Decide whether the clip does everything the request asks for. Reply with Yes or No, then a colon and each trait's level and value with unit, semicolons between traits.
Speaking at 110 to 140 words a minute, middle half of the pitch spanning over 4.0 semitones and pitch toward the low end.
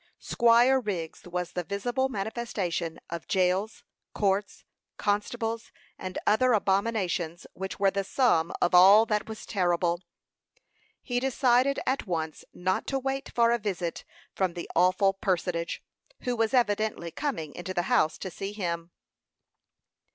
No: slow, 135 wpm; average, 4.7 semitones; high, 200 Hz